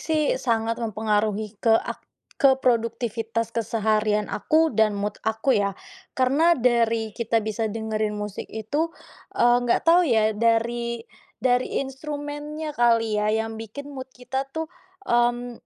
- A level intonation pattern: No, average, 3.1 semitones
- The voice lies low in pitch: No, high, 230 Hz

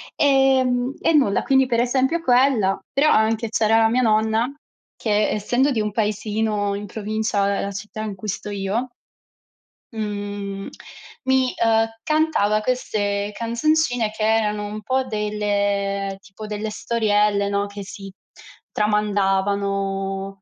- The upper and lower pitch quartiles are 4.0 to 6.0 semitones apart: No, average, 2.8 semitones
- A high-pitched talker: Yes, high, 215 Hz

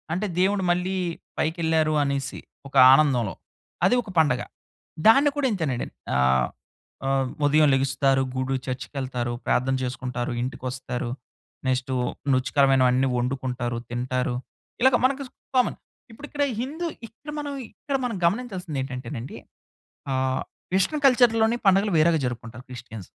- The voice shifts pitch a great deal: Yes, wide, 7.4 semitones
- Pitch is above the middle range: No, low, 135 Hz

